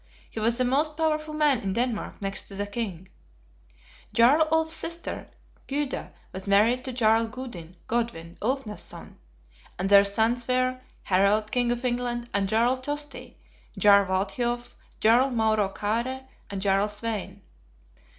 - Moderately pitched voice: No, high, 230 Hz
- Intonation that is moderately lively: Yes, average, 4.1 semitones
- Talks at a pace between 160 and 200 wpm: No, average, 140 wpm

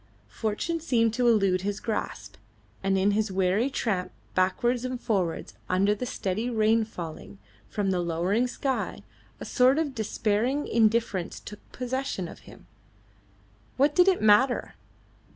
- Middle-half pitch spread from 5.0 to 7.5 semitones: No, average, 4.5 semitones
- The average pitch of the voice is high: Yes, high, 220 Hz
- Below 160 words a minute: Yes, average, 140 wpm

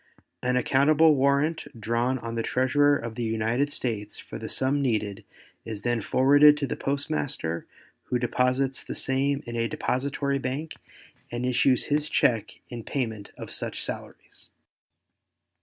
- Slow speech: No, average, 145 wpm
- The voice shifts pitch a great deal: No, average, 3.3 semitones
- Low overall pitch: Yes, low, 130 Hz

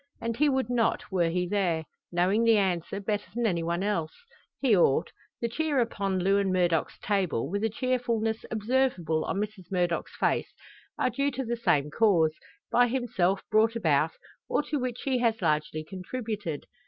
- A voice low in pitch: No, high, 205 Hz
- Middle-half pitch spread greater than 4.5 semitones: Yes, average, 5.1 semitones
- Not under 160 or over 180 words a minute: Yes, average, 165 wpm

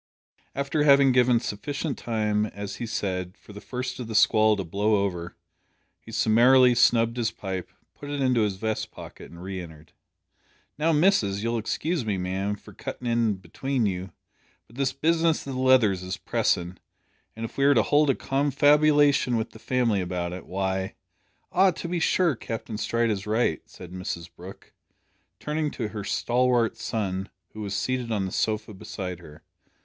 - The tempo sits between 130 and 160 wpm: No, average, 180 wpm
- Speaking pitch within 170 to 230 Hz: No, low, 110 Hz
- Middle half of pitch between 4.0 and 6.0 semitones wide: Yes, average, 5.2 semitones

